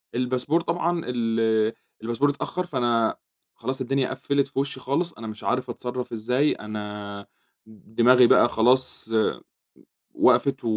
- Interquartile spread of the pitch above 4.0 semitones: No, average, 3.3 semitones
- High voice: No, low, 125 Hz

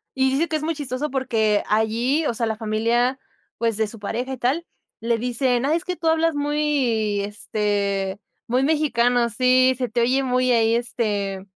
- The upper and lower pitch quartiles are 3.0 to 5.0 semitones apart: Yes, average, 3.5 semitones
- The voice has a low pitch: No, high, 245 Hz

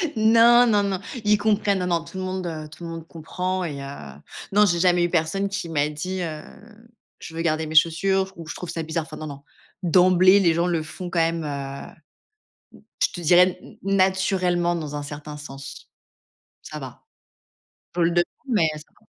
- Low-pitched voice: No, medium, 175 Hz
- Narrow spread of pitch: No, average, 3.0 semitones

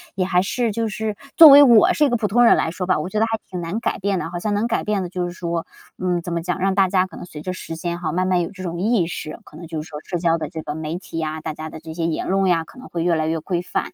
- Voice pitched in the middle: Yes, medium, 180 Hz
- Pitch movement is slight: No, average, 3.4 semitones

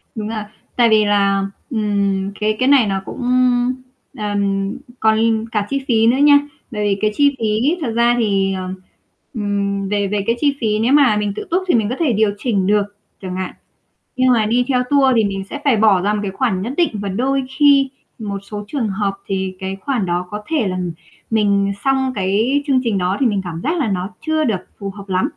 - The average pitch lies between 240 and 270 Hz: No, high, 215 Hz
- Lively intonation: No, average, 4.2 semitones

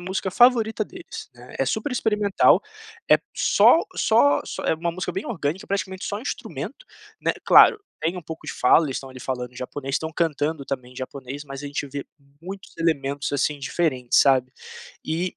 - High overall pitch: No, medium, 160 Hz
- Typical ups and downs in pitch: No, wide, 6.0 semitones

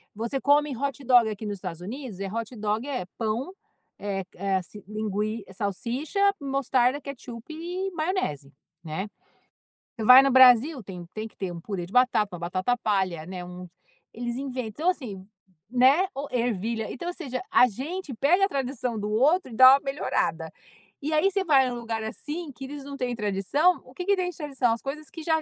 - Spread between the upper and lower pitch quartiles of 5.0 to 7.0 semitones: Yes, average, 5.3 semitones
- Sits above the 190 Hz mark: Yes, high, 245 Hz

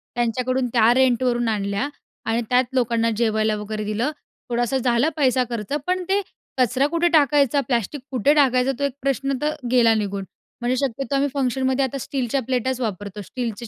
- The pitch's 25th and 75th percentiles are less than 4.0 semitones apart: Yes, average, 3.1 semitones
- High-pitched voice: Yes, very high, 250 Hz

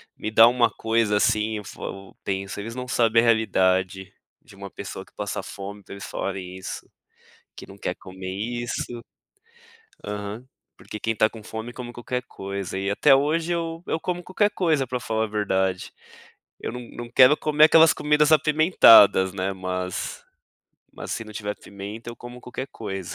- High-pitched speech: No, low, 110 Hz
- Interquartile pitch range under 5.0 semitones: Yes, average, 4.4 semitones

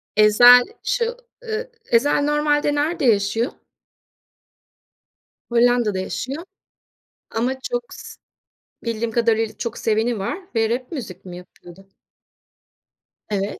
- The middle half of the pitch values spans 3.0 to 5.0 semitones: No, wide, 5.5 semitones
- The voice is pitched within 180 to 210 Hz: No, high, 235 Hz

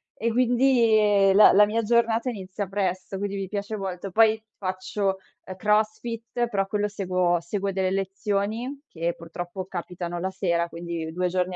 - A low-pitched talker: No, high, 195 Hz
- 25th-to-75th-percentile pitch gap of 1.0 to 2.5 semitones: No, average, 2.9 semitones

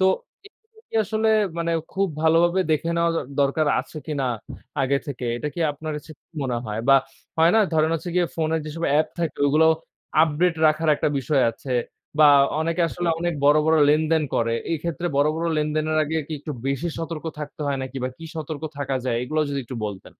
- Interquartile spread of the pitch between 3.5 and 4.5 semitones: No, average, 2.7 semitones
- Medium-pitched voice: Yes, medium, 155 Hz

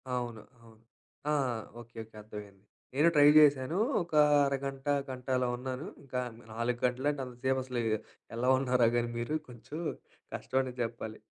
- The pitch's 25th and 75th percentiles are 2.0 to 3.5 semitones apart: Yes, narrow, 2.5 semitones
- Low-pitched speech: Yes, low, 125 Hz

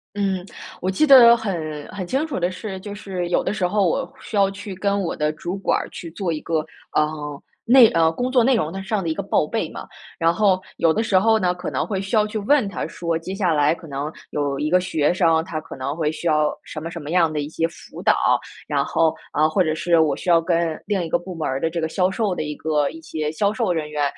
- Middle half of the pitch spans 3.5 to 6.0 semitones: Yes, average, 4.1 semitones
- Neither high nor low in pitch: Yes, medium, 175 Hz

